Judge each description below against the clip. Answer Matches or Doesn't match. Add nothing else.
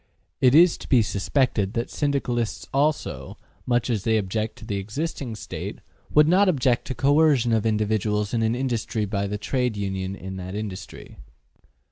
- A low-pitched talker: Matches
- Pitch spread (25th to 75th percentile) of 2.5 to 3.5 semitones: Doesn't match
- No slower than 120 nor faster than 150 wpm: Doesn't match